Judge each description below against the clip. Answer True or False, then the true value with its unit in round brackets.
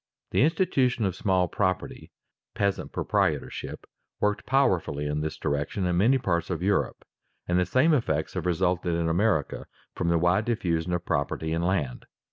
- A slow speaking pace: False (165 wpm)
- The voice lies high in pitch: False (90 Hz)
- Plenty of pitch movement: False (4.0 semitones)